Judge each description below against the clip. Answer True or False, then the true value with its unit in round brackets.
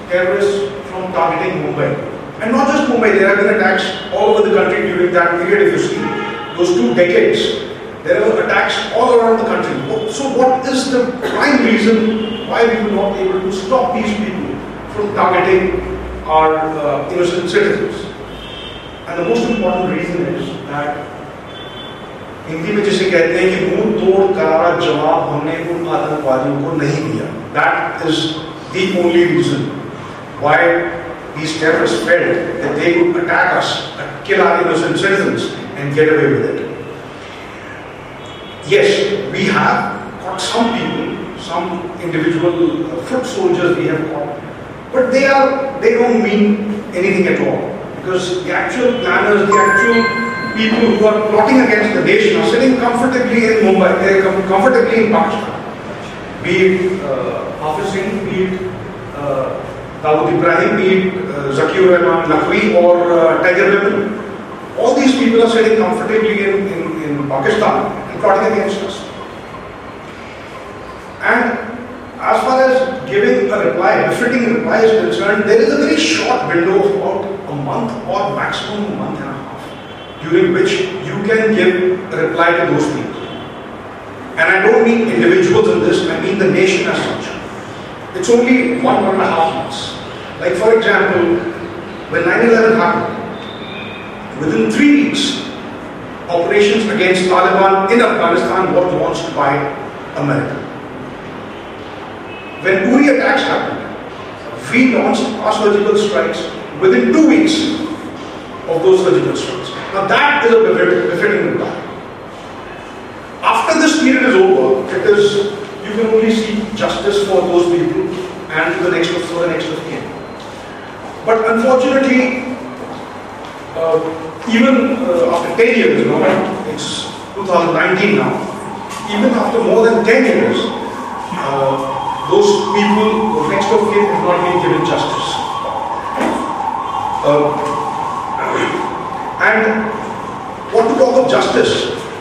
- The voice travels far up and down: True (5.8 semitones)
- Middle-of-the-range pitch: False (205 Hz)